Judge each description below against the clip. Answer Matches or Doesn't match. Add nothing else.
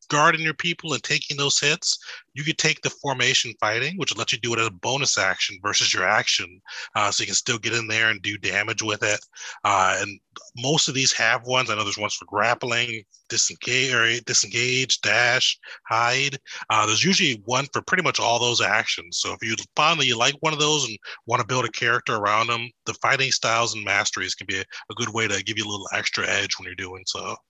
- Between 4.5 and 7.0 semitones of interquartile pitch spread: Doesn't match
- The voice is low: Matches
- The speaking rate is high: Matches